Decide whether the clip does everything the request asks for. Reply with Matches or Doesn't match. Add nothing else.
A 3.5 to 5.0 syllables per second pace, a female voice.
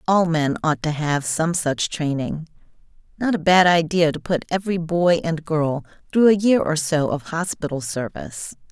Matches